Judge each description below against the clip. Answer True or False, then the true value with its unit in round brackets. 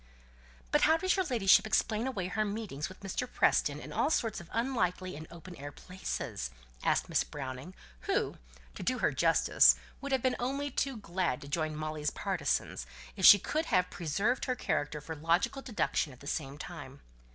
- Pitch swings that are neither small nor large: False (7.7 semitones)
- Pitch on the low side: False (185 Hz)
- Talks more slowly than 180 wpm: False (185 wpm)